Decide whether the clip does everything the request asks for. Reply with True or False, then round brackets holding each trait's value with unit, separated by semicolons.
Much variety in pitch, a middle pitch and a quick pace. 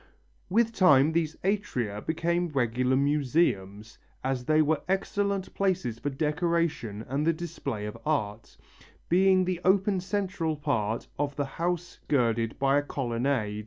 False (6.2 semitones; 150 Hz; 135 wpm)